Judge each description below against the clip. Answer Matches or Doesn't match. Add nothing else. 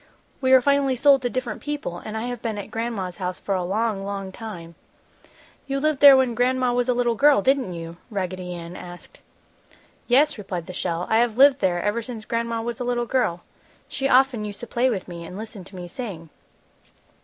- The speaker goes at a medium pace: Doesn't match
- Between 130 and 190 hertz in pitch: Doesn't match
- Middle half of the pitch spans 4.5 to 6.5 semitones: Matches